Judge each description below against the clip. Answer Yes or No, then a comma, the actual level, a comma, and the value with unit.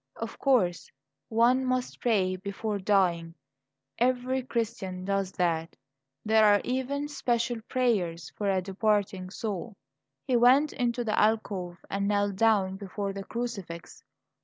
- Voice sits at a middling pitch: No, high, 210 Hz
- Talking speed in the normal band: No, slow, 130 wpm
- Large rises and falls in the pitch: No, average, 4.1 semitones